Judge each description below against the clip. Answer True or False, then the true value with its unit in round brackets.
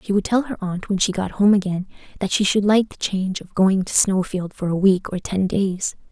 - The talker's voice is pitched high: True (195 Hz)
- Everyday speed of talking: False (255 wpm)